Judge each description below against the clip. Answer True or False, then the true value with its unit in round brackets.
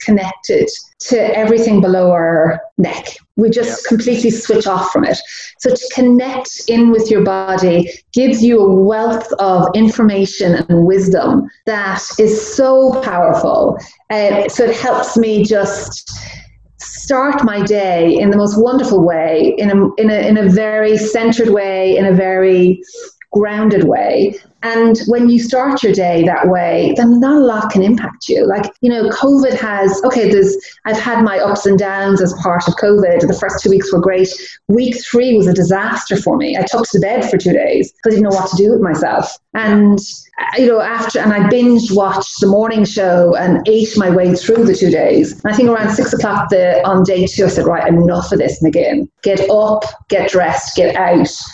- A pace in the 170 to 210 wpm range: True (190 wpm)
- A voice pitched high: True (210 Hz)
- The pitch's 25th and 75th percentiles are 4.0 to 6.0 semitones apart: False (3.4 semitones)